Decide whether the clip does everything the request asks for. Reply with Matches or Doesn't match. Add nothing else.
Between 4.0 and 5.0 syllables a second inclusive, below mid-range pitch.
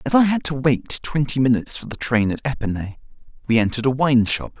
Doesn't match